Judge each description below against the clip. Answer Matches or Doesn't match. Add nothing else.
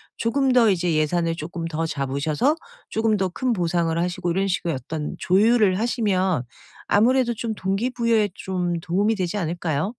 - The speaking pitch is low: Doesn't match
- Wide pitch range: Doesn't match